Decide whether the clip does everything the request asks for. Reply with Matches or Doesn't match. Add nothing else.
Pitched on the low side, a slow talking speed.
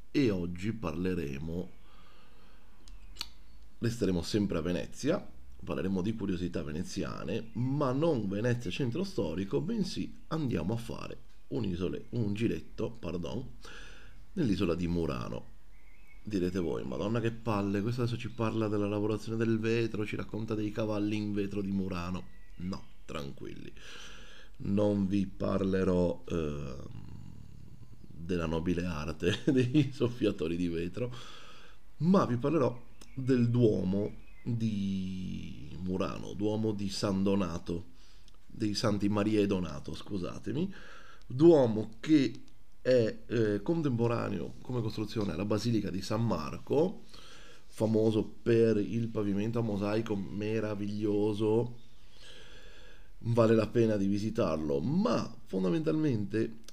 Matches